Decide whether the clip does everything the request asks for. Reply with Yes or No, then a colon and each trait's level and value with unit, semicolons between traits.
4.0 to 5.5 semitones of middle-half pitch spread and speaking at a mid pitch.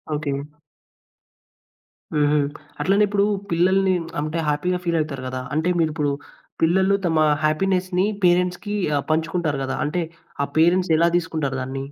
No: average, 3.4 semitones; medium, 165 Hz